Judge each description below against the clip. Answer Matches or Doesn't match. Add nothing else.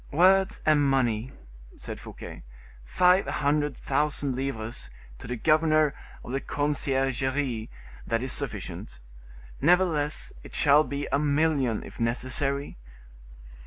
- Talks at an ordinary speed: Doesn't match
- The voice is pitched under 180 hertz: Matches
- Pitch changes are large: Doesn't match